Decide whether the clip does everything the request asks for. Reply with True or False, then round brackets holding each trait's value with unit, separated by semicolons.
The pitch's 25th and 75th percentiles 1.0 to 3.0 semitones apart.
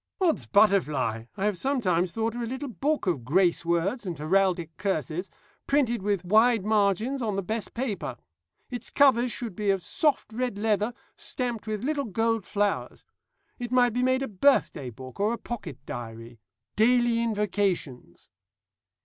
False (5.1 semitones)